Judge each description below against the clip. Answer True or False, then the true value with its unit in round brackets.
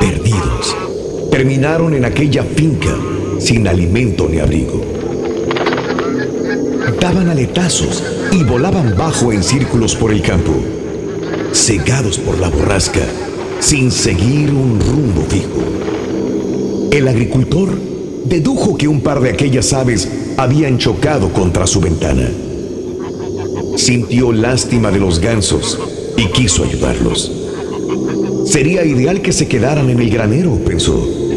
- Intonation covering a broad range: True (6.5 semitones)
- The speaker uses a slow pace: True (110 wpm)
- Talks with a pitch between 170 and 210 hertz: False (120 Hz)